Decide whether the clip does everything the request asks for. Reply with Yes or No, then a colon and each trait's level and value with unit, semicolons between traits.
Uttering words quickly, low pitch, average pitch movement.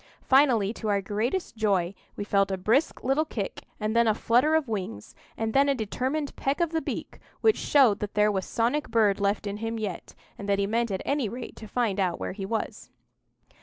No: fast, 215 wpm; high, 220 Hz; average, 4.2 semitones